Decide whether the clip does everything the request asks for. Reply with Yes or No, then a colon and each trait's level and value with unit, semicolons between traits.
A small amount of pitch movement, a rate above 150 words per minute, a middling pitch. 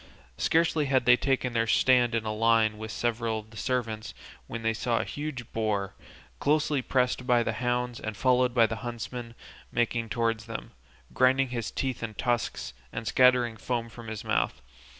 No: narrow, 2.1 semitones; average, 175 wpm; low, 120 Hz